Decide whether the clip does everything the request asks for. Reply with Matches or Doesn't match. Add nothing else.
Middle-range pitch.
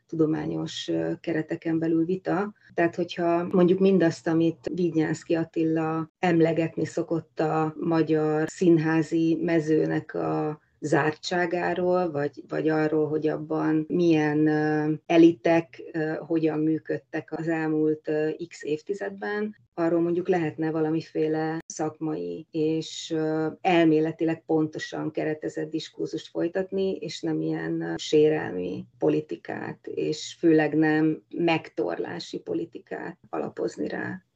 Matches